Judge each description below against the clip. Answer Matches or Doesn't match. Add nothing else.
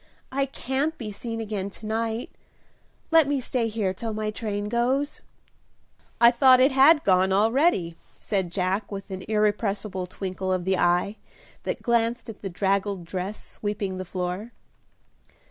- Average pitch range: Matches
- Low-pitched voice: Doesn't match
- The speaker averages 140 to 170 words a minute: Matches